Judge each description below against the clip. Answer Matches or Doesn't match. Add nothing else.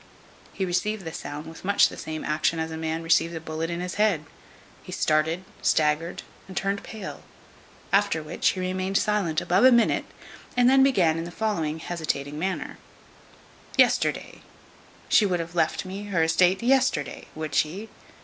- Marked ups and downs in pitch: Doesn't match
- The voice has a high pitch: Doesn't match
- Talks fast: Doesn't match